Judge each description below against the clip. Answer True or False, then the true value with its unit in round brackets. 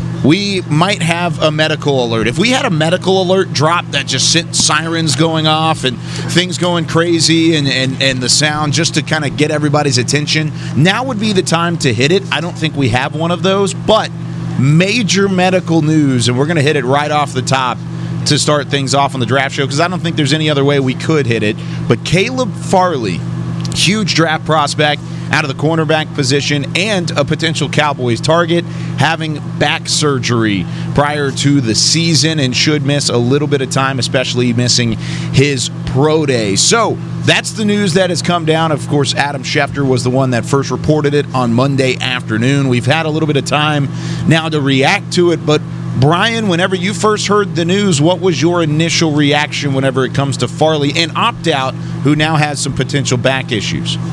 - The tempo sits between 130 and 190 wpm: False (205 wpm)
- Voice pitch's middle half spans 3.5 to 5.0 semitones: False (3.1 semitones)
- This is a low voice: False (150 Hz)